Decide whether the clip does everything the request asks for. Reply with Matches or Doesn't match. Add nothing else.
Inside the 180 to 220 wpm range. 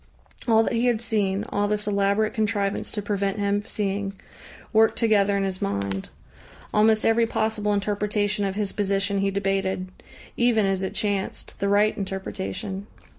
Doesn't match